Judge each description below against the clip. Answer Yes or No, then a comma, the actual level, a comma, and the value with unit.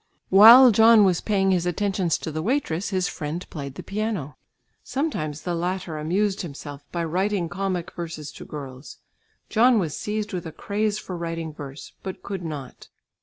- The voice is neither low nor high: Yes, medium, 180 Hz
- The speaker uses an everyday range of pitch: Yes, average, 4.5 semitones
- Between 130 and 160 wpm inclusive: No, average, 170 wpm